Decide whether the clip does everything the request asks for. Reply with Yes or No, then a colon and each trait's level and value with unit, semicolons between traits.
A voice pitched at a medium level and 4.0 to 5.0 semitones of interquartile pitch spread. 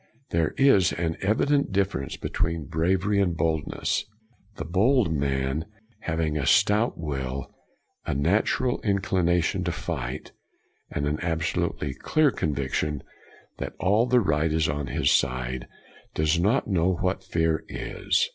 No: very low, 85 Hz; average, 4.6 semitones